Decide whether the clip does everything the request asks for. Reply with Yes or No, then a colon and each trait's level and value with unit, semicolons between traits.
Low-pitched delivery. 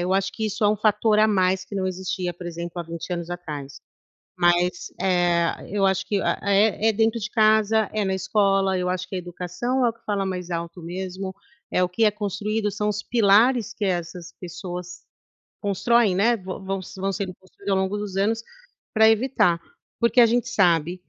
No: high, 195 Hz